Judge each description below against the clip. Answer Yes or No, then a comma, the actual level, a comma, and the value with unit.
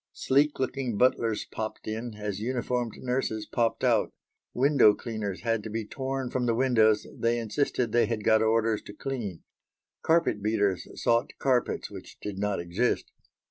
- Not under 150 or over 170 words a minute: Yes, average, 155 wpm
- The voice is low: Yes, low, 115 Hz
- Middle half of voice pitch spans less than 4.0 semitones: Yes, average, 2.9 semitones